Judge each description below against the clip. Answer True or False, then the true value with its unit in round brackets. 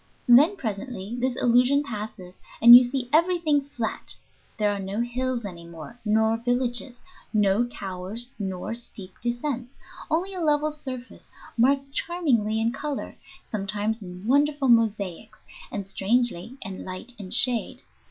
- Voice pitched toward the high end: True (235 Hz)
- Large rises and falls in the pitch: False (4.3 semitones)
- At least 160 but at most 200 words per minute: False (135 wpm)